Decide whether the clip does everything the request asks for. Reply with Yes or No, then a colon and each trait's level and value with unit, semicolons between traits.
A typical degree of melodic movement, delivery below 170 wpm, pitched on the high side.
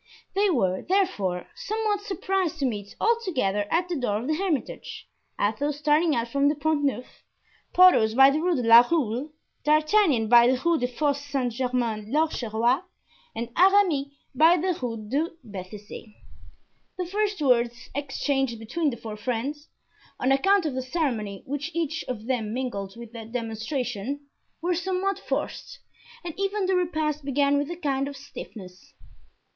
No: wide, 6.1 semitones; average, 160 wpm; very high, 275 Hz